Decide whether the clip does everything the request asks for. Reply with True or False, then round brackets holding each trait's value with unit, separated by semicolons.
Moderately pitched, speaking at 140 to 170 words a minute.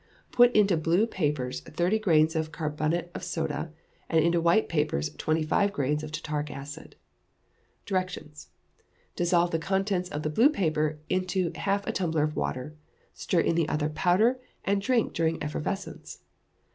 True (165 Hz; 155 wpm)